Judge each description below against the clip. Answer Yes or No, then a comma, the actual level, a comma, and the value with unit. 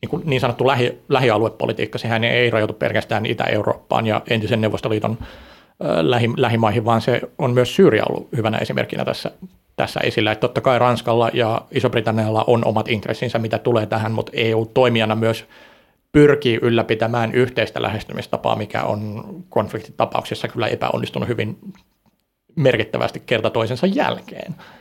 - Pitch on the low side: Yes, low, 115 Hz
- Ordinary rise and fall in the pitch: No, narrow, 1.8 semitones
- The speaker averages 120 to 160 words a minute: Yes, average, 130 wpm